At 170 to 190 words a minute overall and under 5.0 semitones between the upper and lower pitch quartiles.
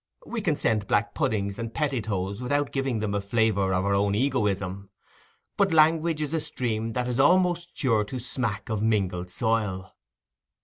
No: average, 175 wpm; wide, 5.6 semitones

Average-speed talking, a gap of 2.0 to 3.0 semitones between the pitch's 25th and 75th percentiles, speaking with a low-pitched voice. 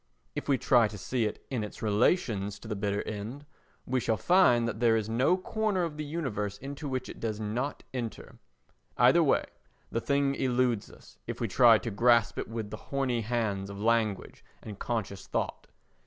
No: average, 190 wpm; average, 3.8 semitones; low, 115 Hz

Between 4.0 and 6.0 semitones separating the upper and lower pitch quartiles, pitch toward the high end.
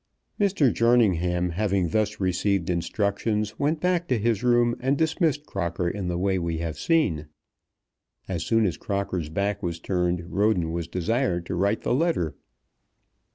No: average, 5.3 semitones; low, 100 Hz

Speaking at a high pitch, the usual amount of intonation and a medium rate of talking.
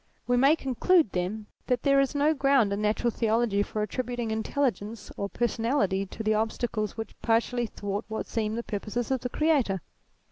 Yes: high, 225 Hz; average, 3.2 semitones; average, 180 wpm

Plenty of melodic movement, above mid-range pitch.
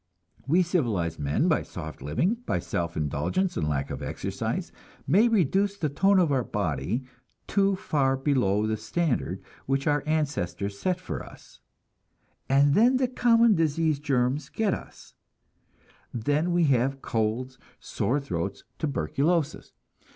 No: wide, 8.4 semitones; medium, 140 Hz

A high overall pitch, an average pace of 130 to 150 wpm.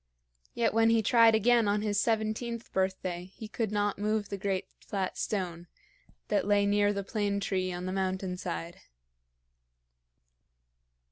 Yes: high, 205 Hz; average, 145 wpm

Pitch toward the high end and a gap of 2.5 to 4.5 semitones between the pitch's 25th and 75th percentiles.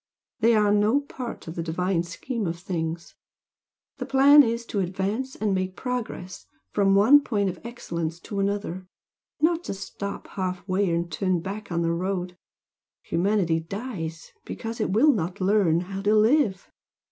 Yes: high, 195 Hz; average, 3.9 semitones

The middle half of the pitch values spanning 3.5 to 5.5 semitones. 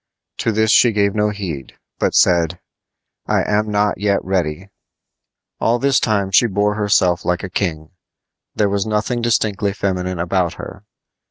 No: narrow, 2.6 semitones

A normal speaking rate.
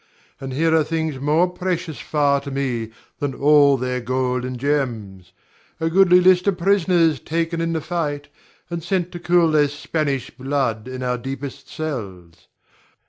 Yes: average, 160 wpm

